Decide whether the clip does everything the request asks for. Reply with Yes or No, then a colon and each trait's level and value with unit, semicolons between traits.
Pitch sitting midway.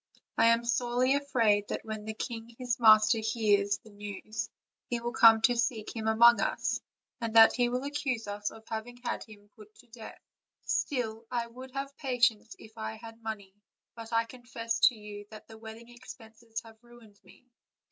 No: high, 225 Hz